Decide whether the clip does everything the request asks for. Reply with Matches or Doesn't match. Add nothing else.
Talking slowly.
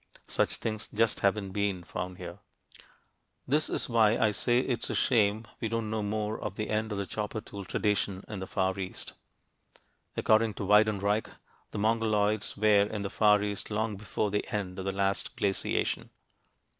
Doesn't match